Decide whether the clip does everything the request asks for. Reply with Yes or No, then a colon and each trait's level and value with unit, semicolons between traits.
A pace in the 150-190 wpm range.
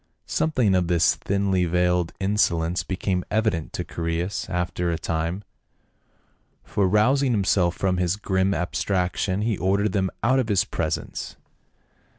No: slow, 135 wpm